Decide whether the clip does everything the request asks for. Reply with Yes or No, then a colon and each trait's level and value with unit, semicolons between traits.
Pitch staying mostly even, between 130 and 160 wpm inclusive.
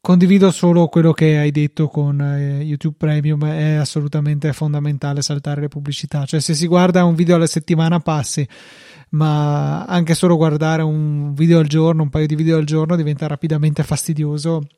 No: narrow, 1.8 semitones; fast, 170 wpm